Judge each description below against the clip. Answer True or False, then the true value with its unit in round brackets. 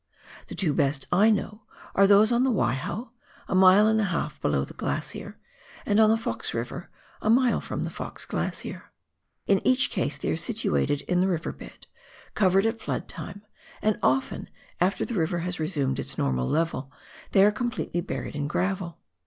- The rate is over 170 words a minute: True (185 wpm)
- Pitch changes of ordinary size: False (6.1 semitones)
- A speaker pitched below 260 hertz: True (185 Hz)